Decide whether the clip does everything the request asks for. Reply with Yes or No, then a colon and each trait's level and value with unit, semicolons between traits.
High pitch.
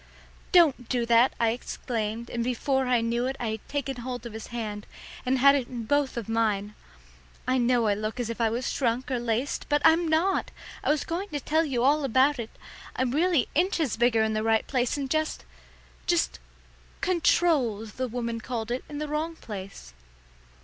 Yes: high, 245 Hz